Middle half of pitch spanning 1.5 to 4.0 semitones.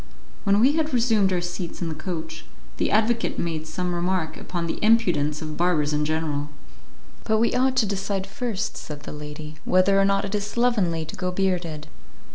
No: average, 4.7 semitones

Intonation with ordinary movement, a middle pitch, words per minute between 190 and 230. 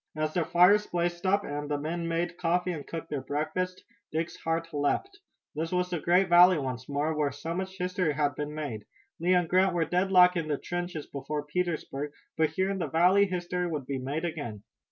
Yes: average, 3.3 semitones; medium, 165 Hz; fast, 205 wpm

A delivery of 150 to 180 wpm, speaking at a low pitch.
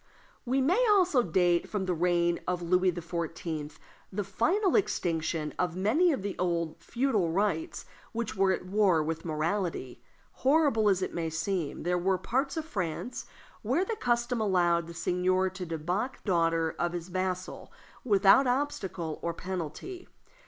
No: average, 155 wpm; medium, 185 Hz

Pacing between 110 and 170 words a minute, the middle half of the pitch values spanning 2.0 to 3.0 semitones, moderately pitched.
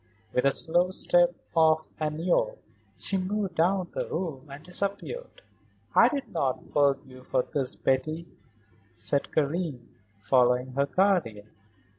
No: slow, 135 wpm; wide, 5.4 semitones; medium, 155 Hz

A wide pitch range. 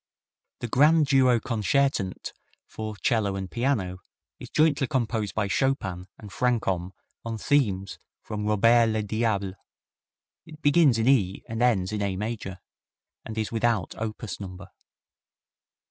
No: average, 4.0 semitones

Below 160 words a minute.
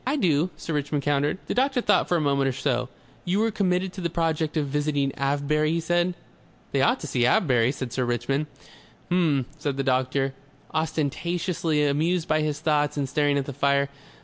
No: average, 195 wpm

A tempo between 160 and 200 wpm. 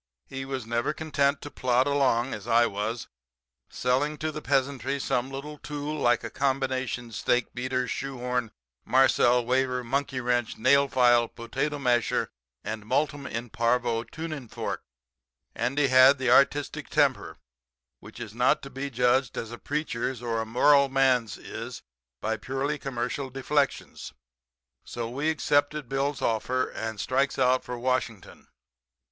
No: average, 145 wpm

